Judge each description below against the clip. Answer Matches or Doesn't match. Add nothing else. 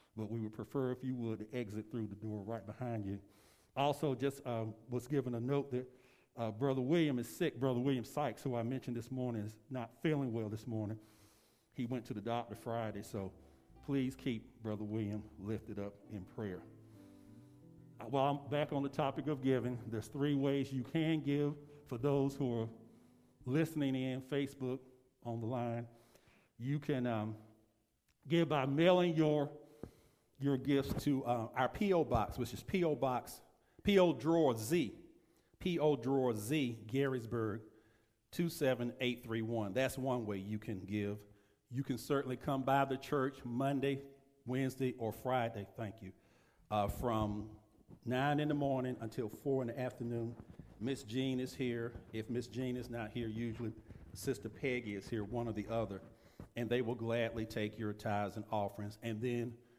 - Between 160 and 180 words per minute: Matches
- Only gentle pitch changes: Doesn't match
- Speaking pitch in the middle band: Doesn't match